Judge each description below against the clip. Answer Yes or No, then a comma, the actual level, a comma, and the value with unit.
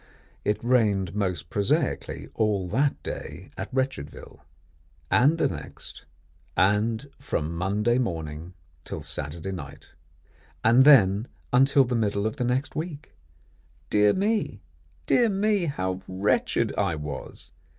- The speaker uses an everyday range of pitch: No, wide, 6.4 semitones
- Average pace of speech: No, slow, 120 wpm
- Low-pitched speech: Yes, low, 105 Hz